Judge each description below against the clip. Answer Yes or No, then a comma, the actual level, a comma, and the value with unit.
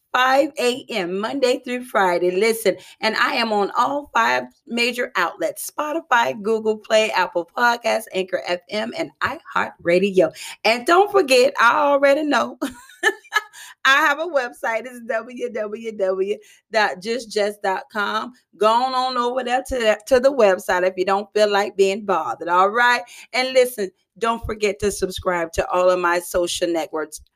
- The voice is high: Yes, high, 220 Hz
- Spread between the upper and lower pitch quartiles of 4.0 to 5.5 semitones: Yes, average, 5.2 semitones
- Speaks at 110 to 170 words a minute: Yes, average, 140 wpm